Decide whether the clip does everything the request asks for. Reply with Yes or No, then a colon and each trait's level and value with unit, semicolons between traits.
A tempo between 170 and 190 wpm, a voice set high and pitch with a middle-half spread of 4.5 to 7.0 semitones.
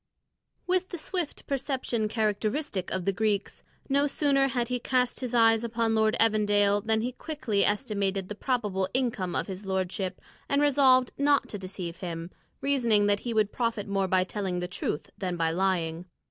Yes: average, 175 wpm; high, 215 Hz; average, 4.8 semitones